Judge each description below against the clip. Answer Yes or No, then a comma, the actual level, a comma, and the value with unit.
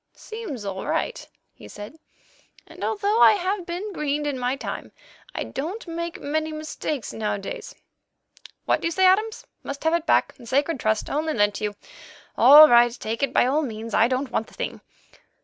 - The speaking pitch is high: Yes, very high, 295 Hz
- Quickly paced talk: No, average, 185 wpm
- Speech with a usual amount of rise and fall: No, wide, 6.2 semitones